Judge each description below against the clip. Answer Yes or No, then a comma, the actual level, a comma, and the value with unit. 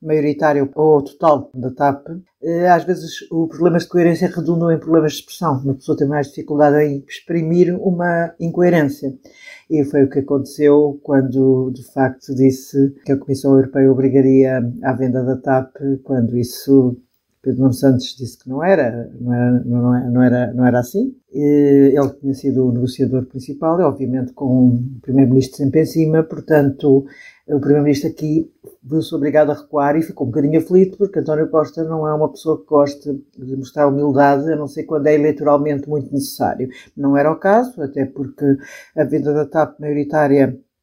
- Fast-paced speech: No, average, 170 wpm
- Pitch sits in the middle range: Yes, medium, 145 Hz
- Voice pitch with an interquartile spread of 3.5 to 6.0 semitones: No, average, 2.7 semitones